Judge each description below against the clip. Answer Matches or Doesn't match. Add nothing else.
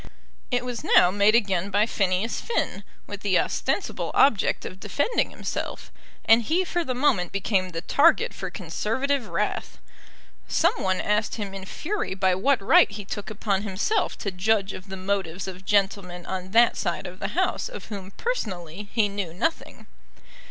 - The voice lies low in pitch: Doesn't match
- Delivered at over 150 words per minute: Matches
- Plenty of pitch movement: Doesn't match